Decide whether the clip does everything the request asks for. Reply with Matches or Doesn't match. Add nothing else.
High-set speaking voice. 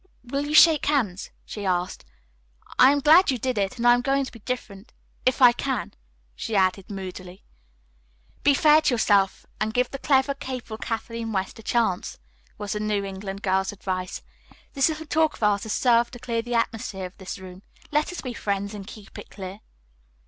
Matches